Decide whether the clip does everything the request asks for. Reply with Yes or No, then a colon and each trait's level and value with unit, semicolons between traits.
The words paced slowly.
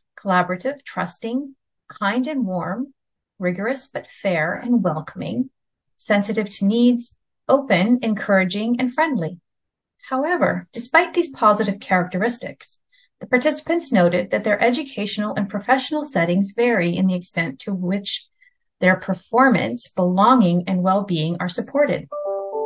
Yes: slow, 120 wpm